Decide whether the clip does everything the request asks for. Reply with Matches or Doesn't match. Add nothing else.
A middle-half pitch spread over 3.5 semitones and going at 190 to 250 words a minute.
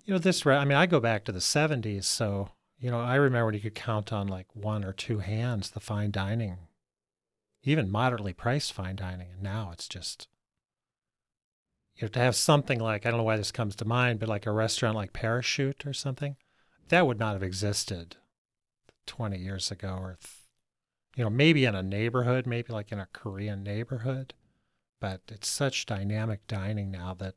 Matches